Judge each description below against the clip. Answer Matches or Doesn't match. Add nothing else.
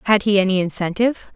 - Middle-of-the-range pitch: Doesn't match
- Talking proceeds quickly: Doesn't match